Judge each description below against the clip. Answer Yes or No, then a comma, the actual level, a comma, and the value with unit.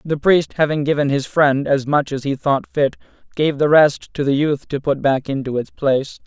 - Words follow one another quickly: Yes, fast, 230 wpm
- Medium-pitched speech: Yes, medium, 145 Hz